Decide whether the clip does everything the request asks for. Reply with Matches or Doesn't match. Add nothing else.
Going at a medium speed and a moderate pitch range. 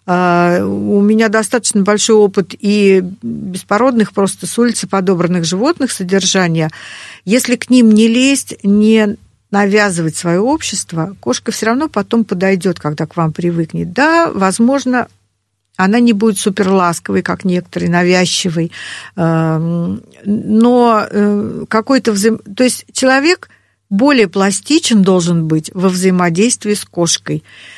Matches